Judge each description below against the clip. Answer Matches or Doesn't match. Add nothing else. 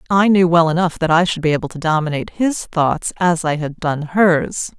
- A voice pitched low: Doesn't match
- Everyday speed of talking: Doesn't match